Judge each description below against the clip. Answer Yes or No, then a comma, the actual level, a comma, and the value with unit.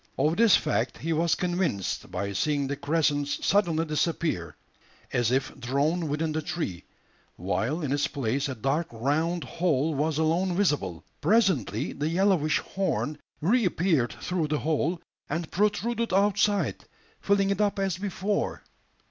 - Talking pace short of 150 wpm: Yes, average, 140 wpm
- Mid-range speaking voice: Yes, medium, 160 Hz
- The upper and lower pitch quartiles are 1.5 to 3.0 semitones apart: No, average, 4.6 semitones